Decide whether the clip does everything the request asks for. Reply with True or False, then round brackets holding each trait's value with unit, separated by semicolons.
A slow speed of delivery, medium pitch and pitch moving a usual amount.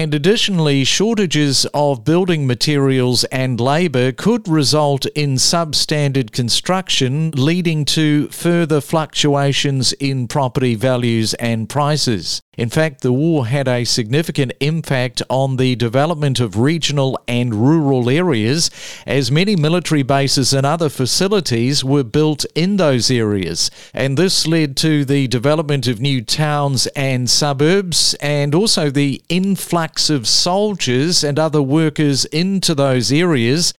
True (130 wpm; 145 Hz; 3.6 semitones)